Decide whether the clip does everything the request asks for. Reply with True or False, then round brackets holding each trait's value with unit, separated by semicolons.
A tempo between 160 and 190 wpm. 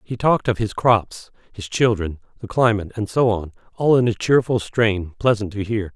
False (200 wpm)